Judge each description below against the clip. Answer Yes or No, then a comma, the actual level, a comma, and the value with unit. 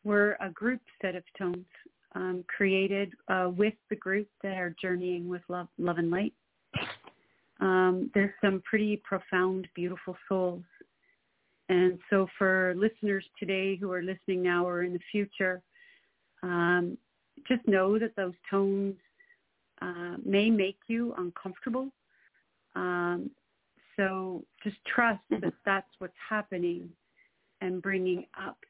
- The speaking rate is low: Yes, slow, 130 wpm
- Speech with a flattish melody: Yes, narrow, 2.3 semitones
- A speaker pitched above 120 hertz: Yes, high, 190 Hz